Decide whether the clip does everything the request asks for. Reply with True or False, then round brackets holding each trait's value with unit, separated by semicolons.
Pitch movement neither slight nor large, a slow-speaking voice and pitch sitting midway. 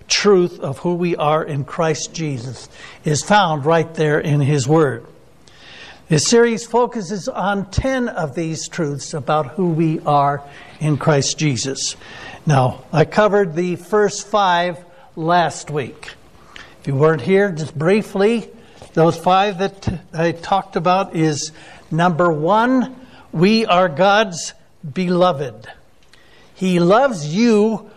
True (4.4 semitones; 130 wpm; 175 Hz)